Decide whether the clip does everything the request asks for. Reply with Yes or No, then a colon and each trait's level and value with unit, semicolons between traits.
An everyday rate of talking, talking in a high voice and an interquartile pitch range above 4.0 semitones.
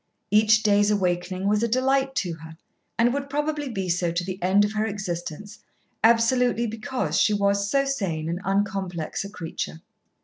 Yes: average, 170 wpm; high, 205 Hz; average, 4.4 semitones